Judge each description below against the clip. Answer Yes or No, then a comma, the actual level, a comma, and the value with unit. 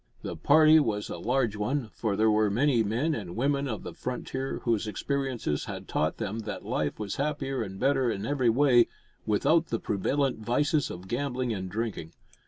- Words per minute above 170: Yes, average, 185 wpm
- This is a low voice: Yes, low, 120 Hz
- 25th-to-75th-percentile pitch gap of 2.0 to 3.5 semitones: No, average, 4.8 semitones